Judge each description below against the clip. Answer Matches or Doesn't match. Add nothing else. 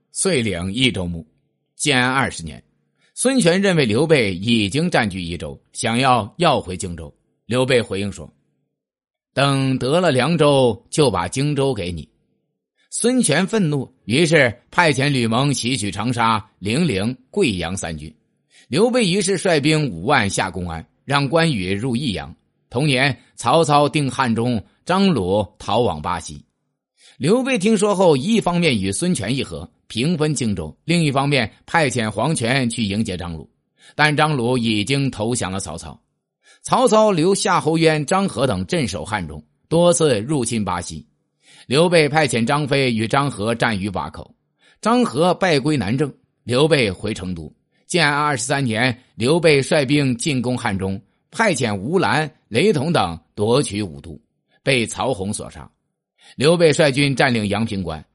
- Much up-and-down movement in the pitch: Matches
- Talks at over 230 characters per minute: Doesn't match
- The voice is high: Doesn't match